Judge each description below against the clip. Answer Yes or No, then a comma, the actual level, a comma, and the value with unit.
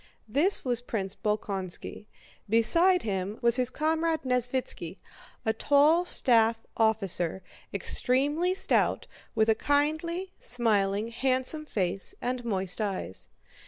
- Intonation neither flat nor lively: No, wide, 5.7 semitones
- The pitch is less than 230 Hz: No, high, 240 Hz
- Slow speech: Yes, slow, 110 wpm